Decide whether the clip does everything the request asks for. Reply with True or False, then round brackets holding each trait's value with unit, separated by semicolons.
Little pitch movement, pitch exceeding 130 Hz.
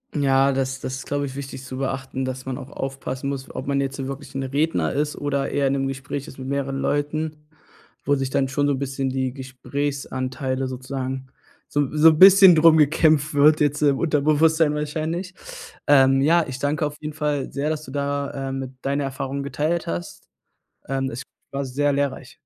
True (1.9 semitones; 140 Hz)